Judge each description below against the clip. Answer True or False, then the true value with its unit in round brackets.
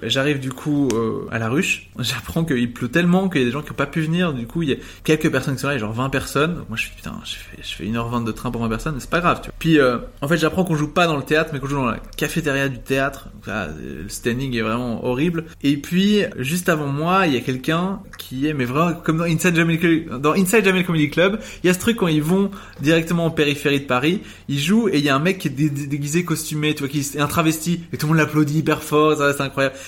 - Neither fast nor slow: False (290 wpm)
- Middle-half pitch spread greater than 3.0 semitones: True (4.0 semitones)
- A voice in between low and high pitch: True (150 Hz)